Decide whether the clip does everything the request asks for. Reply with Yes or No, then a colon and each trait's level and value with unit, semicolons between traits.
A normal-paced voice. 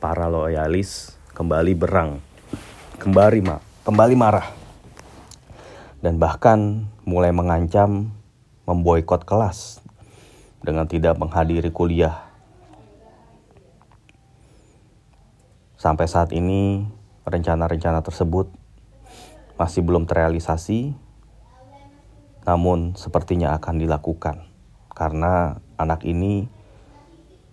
No: slow, 70 wpm